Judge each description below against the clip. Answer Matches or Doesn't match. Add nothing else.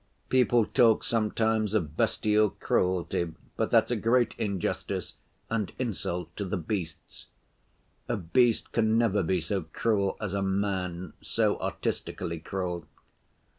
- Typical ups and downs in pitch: Matches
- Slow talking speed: Matches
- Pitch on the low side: Matches